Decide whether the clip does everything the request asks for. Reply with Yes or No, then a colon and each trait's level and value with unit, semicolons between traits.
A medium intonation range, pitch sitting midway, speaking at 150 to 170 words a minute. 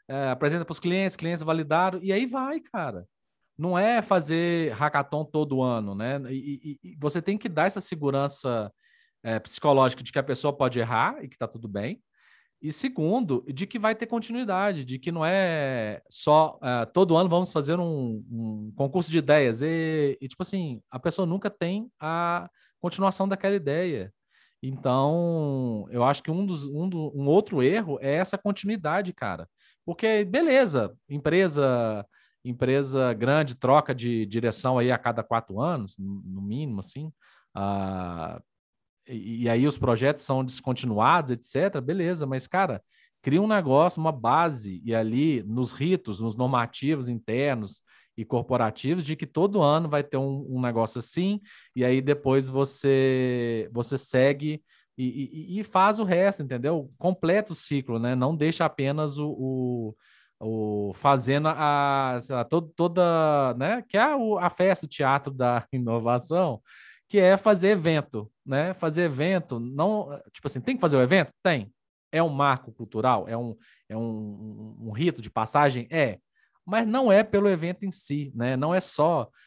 No: wide, 6.0 semitones; medium, 145 Hz; average, 165 wpm